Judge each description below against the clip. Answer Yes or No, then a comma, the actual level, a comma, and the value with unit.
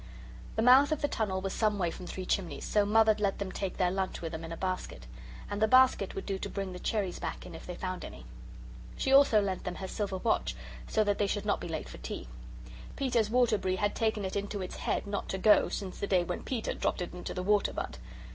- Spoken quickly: Yes, fast, 250 wpm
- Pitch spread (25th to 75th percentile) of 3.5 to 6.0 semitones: No, average, 2.7 semitones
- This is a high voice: Yes, high, 195 Hz